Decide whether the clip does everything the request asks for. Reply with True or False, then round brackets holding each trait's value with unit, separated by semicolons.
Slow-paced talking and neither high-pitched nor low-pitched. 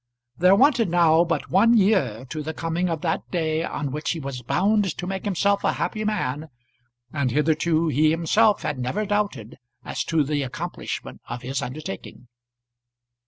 False (165 wpm; 165 Hz)